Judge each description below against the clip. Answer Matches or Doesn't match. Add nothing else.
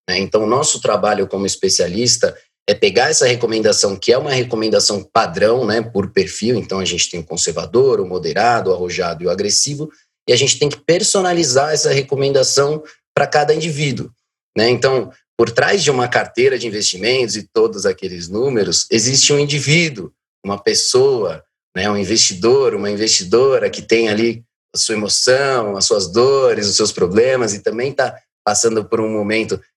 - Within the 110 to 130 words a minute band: Doesn't match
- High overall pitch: Doesn't match